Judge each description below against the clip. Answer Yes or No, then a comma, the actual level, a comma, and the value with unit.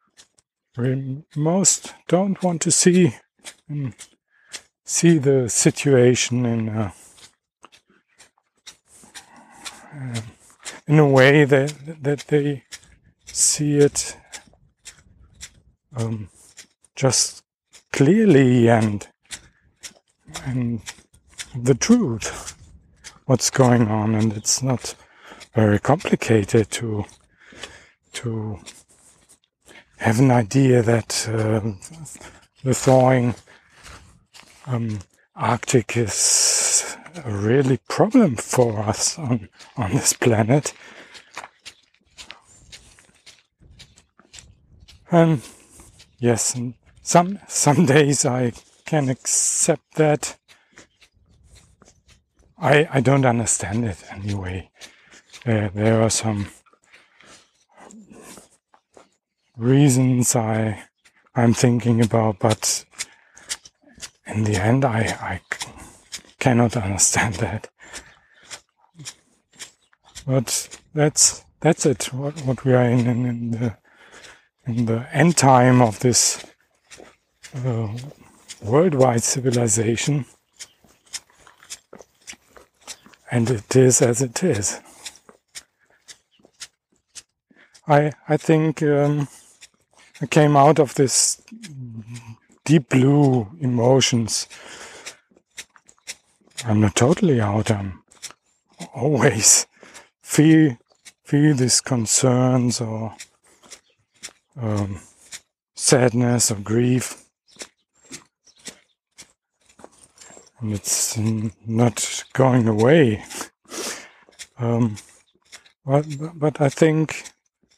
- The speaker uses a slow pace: Yes, slow, 80 wpm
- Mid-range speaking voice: No, low, 120 Hz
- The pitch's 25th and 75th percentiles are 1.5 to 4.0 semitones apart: No, average, 4.4 semitones